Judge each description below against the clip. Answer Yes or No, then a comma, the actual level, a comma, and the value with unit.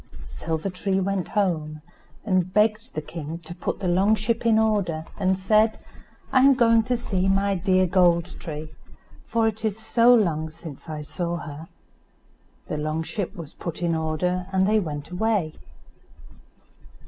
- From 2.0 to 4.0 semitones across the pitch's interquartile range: No, average, 4.8 semitones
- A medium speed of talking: Yes, average, 160 wpm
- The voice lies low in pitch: No, medium, 185 Hz